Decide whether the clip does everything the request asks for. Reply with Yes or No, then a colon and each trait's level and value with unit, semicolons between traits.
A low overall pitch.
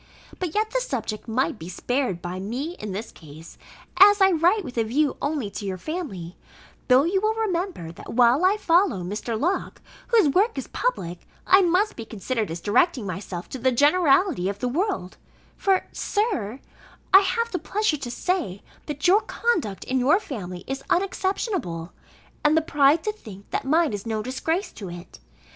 No: very high, 275 Hz